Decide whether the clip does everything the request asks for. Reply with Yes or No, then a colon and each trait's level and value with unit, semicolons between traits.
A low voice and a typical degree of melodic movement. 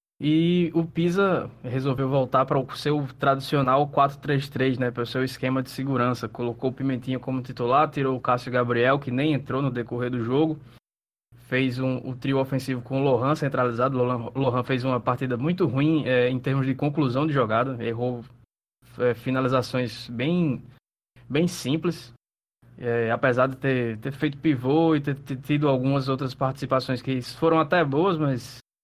No: low, 130 Hz; narrow, 2.3 semitones